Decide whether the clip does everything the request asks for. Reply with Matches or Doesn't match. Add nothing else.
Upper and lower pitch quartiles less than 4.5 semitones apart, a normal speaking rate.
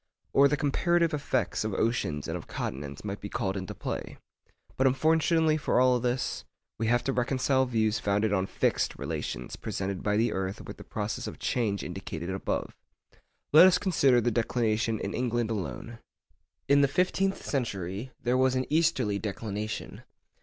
Doesn't match